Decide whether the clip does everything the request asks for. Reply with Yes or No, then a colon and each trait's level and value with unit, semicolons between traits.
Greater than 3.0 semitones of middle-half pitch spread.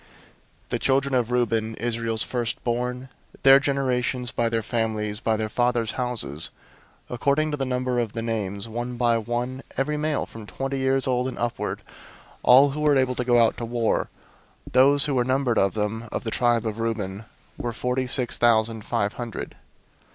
No: narrow, 2.4 semitones